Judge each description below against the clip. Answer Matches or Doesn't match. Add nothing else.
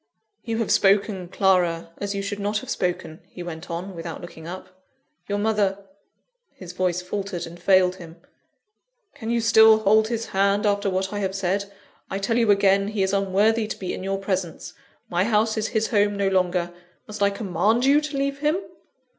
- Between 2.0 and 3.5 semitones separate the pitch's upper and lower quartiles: Matches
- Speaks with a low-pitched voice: Doesn't match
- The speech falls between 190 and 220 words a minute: Matches